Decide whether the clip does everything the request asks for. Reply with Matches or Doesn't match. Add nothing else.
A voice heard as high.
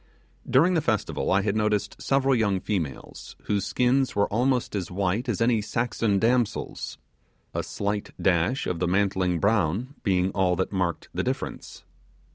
Doesn't match